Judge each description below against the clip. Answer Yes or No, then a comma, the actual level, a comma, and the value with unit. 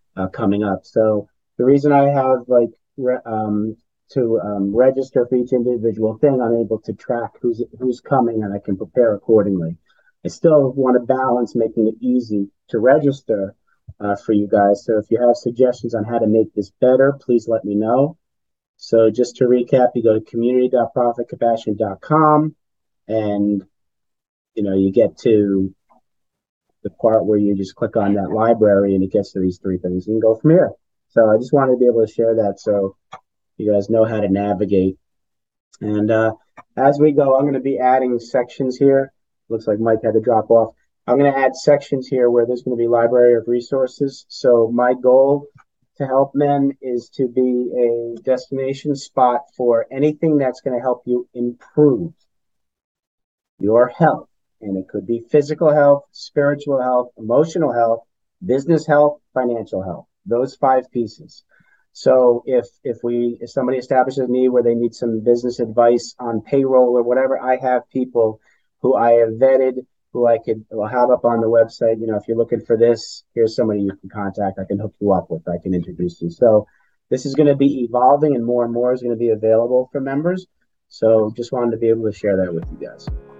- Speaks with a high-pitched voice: No, low, 120 Hz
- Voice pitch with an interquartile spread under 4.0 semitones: Yes, average, 3.0 semitones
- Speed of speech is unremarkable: Yes, average, 195 wpm